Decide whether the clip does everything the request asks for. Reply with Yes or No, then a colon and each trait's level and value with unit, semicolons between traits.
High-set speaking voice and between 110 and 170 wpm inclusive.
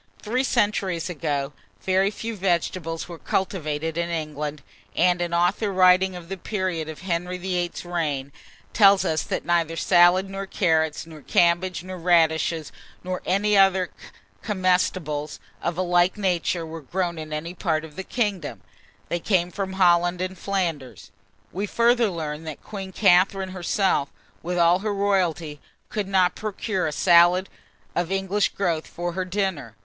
No: medium, 180 Hz; average, 155 wpm